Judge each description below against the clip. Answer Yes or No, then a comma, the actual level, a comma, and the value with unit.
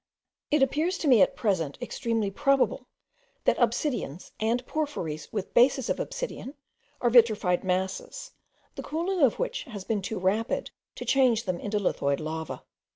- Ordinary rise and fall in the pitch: No, wide, 6.6 semitones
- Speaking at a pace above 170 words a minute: No, average, 155 wpm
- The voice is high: Yes, high, 230 Hz